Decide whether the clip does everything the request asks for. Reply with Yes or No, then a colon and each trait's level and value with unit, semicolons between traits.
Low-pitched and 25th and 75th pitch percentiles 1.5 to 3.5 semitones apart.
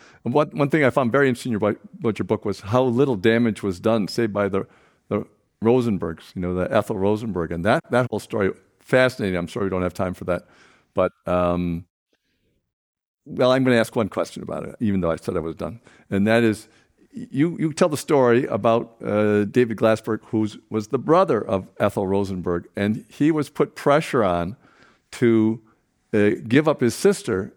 No: low, 110 Hz; average, 4.1 semitones